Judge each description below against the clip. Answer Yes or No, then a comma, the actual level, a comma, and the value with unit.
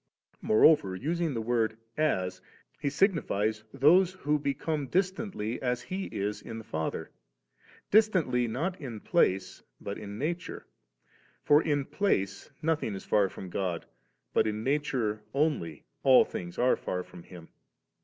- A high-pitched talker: No, low, 125 Hz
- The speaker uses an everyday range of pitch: No, wide, 7.4 semitones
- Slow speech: No, average, 155 wpm